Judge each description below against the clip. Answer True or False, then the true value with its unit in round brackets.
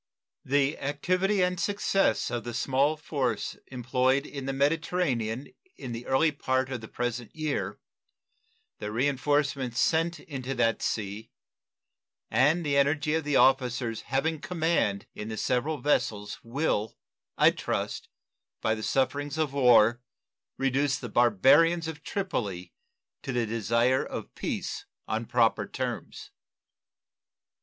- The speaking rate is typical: False (130 wpm)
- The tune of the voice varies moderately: True (4.1 semitones)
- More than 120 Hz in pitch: True (135 Hz)